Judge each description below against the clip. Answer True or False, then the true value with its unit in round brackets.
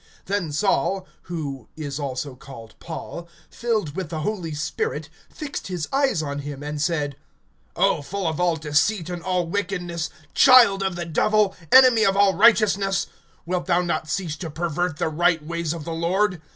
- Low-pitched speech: False (170 Hz)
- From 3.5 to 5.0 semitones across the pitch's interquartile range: True (4.2 semitones)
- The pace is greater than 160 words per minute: True (170 wpm)